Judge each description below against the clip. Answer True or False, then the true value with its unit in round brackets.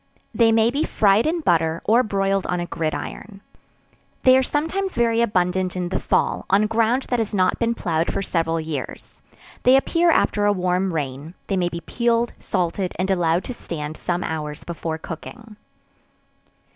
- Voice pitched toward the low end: False (195 Hz)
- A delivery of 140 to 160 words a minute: False (170 wpm)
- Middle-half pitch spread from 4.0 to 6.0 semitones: True (5.4 semitones)